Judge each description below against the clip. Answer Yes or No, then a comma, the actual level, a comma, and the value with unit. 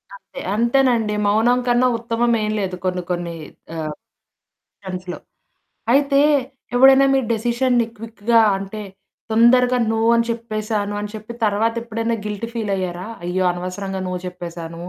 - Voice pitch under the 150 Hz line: No, high, 220 Hz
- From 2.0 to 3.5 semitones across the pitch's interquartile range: No, average, 4.0 semitones